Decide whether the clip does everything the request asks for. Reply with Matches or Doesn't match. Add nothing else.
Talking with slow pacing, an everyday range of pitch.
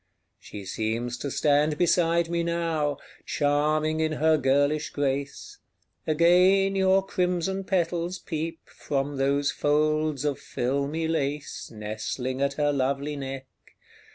Matches